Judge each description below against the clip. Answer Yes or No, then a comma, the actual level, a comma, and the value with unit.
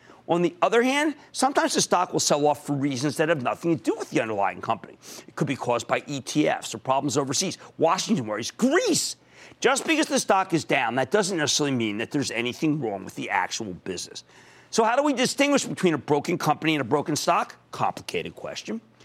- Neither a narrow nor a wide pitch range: No, wide, 6.8 semitones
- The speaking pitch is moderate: Yes, medium, 155 Hz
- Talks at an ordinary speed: No, fast, 210 wpm